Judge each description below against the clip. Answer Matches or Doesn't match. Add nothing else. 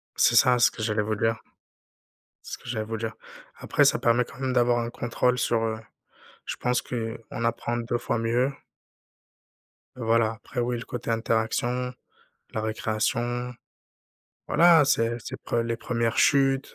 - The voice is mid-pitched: Doesn't match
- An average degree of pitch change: Doesn't match